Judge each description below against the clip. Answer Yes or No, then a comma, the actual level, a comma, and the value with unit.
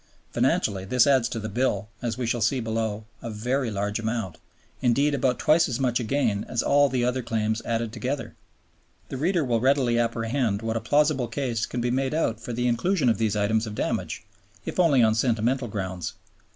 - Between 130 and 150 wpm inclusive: No, average, 195 wpm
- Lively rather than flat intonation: No, average, 2.9 semitones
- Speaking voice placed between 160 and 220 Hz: No, low, 120 Hz